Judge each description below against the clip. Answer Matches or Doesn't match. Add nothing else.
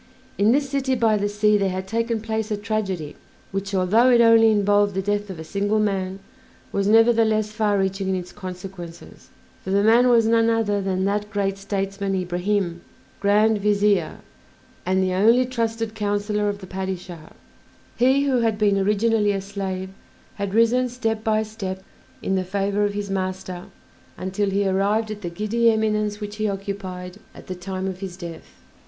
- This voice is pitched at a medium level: Doesn't match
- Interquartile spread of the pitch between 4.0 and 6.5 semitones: Doesn't match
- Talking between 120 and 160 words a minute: Doesn't match